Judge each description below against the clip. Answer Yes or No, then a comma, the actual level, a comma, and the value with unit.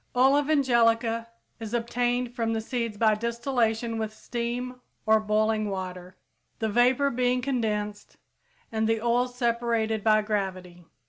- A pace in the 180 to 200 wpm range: No, slow, 135 wpm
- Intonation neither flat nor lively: No, narrow, 2.2 semitones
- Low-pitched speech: No, high, 230 Hz